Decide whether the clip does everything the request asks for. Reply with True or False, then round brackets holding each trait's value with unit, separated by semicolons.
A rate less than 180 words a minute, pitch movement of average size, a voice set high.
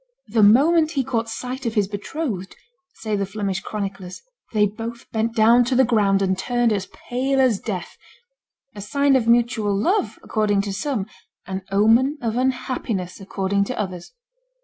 True (165 wpm; 4.1 semitones; 220 Hz)